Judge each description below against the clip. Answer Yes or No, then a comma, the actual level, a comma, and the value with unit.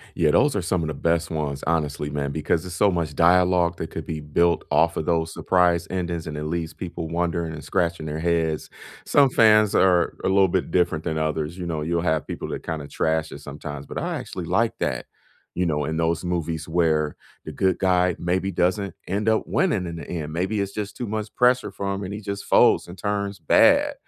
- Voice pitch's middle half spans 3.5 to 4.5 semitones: No, average, 3.0 semitones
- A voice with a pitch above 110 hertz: No, very low, 85 Hz